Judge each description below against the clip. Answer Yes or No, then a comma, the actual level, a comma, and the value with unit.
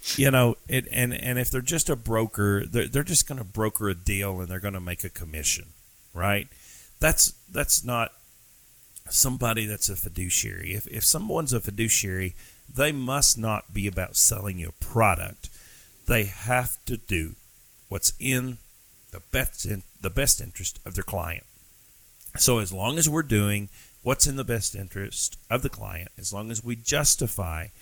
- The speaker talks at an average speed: Yes, average, 175 wpm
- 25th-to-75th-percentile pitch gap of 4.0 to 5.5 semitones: Yes, average, 4.3 semitones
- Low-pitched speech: Yes, low, 110 Hz